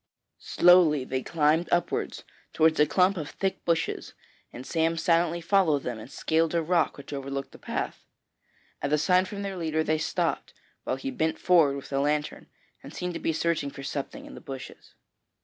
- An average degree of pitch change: Yes, average, 3.3 semitones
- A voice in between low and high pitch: Yes, medium, 160 Hz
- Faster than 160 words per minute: Yes, average, 185 wpm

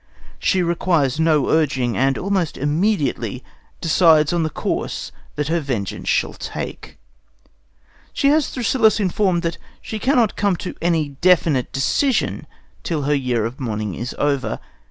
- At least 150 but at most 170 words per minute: No, average, 140 wpm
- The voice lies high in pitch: No, medium, 160 Hz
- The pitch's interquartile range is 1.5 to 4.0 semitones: No, wide, 5.4 semitones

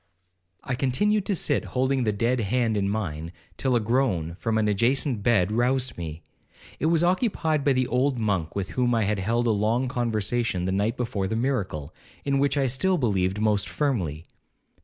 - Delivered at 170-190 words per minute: Yes, average, 185 wpm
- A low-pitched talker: Yes, low, 115 Hz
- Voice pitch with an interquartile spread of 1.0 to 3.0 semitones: No, average, 4.7 semitones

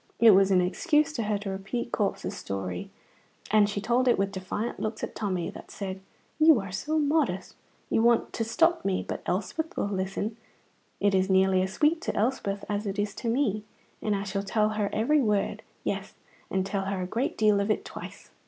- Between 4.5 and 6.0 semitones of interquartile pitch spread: No, average, 3.2 semitones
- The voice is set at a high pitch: Yes, high, 205 Hz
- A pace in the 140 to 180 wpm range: No, fast, 205 wpm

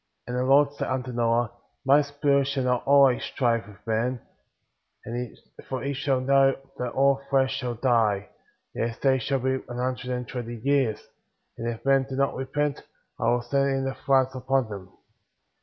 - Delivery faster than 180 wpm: Yes, average, 190 wpm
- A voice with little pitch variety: Yes, narrow, 2.2 semitones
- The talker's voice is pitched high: No, low, 130 Hz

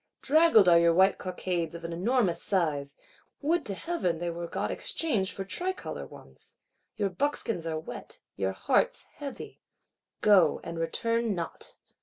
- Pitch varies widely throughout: Yes, wide, 5.7 semitones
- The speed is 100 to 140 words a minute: No, average, 150 wpm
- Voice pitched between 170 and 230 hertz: Yes, medium, 185 Hz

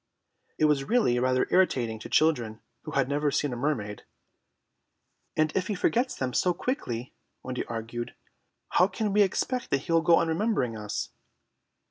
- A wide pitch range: Yes, wide, 7.0 semitones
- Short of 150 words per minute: No, average, 165 wpm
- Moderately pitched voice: Yes, medium, 145 Hz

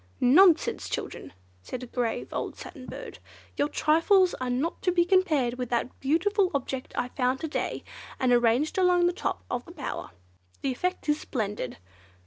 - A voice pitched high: Yes, very high, 285 Hz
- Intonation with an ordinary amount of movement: No, wide, 6.0 semitones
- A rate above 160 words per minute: Yes, average, 170 wpm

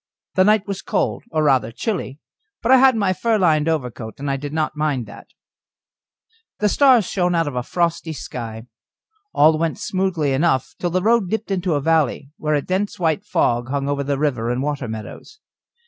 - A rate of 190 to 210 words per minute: Yes, average, 195 wpm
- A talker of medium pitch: Yes, medium, 155 Hz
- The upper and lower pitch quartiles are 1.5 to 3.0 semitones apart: No, wide, 5.4 semitones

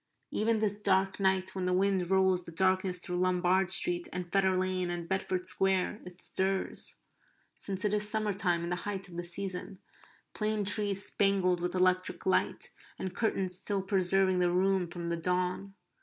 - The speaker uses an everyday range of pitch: No, narrow, 1.4 semitones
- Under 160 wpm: No, average, 175 wpm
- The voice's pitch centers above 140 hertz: Yes, medium, 185 Hz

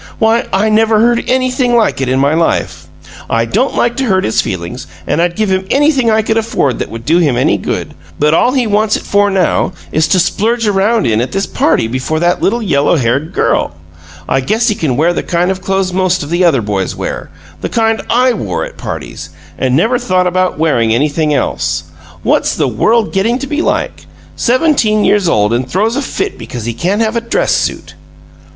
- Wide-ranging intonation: Yes, wide, 7.4 semitones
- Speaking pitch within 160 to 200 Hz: Yes, high, 190 Hz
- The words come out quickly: Yes, fast, 210 wpm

